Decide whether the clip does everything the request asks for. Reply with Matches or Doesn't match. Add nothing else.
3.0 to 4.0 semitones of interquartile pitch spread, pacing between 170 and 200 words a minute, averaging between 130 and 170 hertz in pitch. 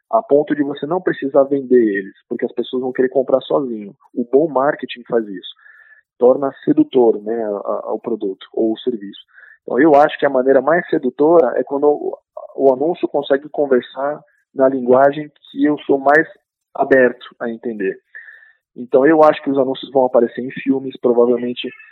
Matches